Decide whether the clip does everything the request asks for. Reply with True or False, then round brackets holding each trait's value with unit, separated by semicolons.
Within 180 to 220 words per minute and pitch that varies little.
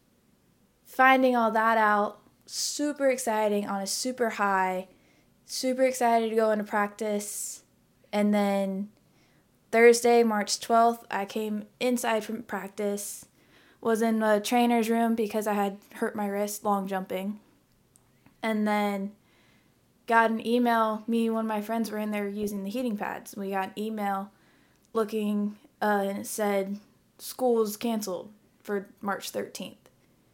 False (140 wpm; 2.1 semitones)